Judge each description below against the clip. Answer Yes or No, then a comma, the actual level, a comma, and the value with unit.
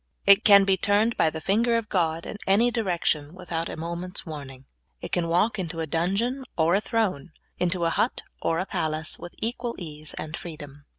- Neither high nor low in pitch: Yes, medium, 175 Hz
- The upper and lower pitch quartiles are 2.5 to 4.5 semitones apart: Yes, average, 4.1 semitones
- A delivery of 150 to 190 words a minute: No, average, 200 wpm